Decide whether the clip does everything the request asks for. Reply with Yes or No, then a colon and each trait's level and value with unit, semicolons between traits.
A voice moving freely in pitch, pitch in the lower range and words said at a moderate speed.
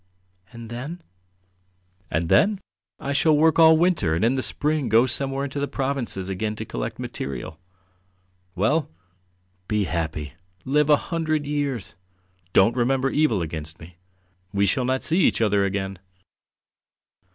Yes: wide, 7.3 semitones; low, 125 Hz; average, 145 wpm